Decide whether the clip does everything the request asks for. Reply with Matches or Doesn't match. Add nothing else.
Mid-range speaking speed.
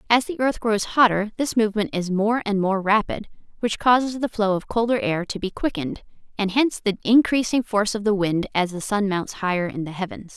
Doesn't match